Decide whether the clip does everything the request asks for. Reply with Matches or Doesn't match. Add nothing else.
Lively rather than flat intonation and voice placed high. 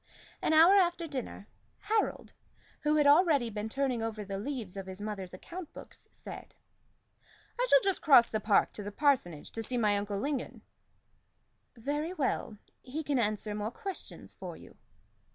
Matches